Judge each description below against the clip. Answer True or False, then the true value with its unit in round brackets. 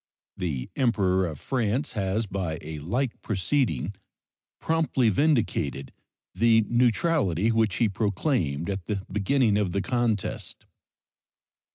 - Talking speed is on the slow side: True (110 wpm)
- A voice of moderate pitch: False (105 Hz)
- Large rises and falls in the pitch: False (4.9 semitones)